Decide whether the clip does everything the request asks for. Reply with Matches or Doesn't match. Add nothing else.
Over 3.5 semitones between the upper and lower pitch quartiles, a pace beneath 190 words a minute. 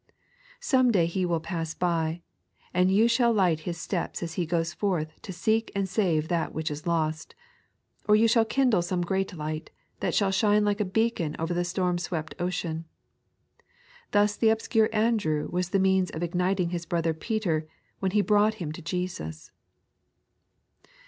Matches